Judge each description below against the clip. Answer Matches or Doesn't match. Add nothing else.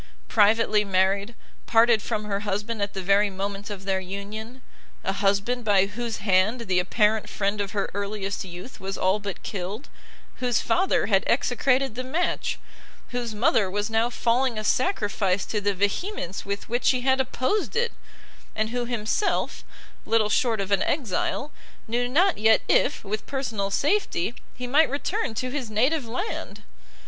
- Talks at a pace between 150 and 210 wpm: Matches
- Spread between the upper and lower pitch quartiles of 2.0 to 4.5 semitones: Matches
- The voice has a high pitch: Matches